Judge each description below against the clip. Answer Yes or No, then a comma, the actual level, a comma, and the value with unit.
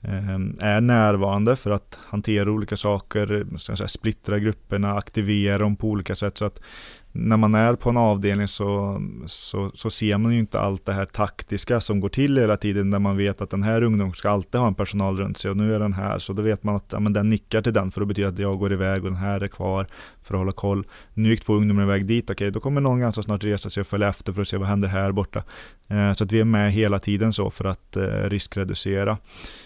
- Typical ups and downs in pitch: No, narrow, 1.5 semitones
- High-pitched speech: No, low, 100 Hz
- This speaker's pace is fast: Yes, fast, 245 wpm